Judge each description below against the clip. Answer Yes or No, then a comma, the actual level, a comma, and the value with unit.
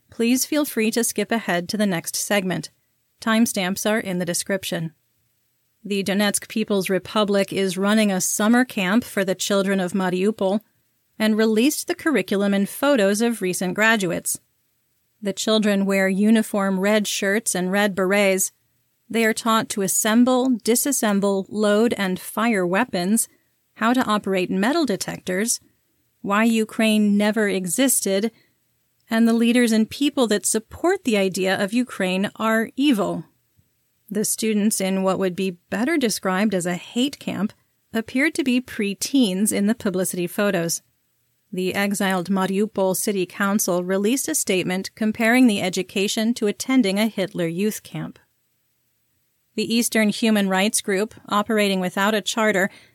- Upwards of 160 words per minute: No, average, 145 wpm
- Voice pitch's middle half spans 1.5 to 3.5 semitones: Yes, average, 2.8 semitones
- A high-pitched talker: Yes, high, 205 Hz